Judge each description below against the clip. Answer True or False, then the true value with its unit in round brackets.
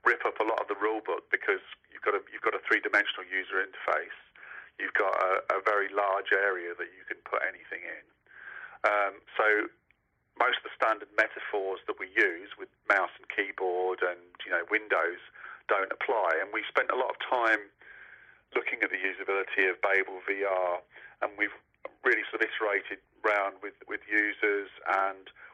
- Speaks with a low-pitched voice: True (100 Hz)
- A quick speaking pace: False (180 wpm)